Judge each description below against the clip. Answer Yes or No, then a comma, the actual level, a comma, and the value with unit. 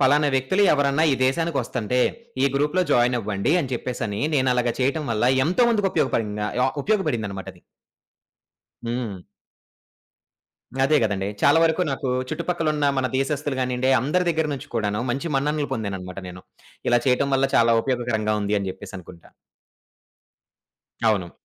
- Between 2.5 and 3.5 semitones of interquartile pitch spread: No, wide, 5.5 semitones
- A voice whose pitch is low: Yes, low, 130 Hz